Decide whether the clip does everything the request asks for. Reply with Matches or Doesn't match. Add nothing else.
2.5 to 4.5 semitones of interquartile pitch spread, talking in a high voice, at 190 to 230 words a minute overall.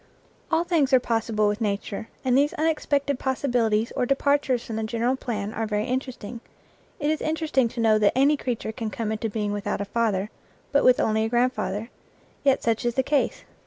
Matches